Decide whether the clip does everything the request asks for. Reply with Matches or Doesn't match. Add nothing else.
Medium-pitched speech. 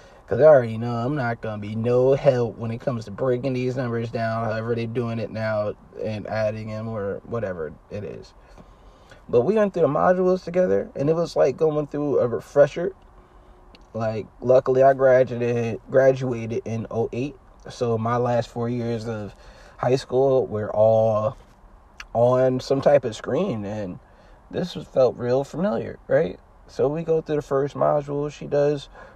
Doesn't match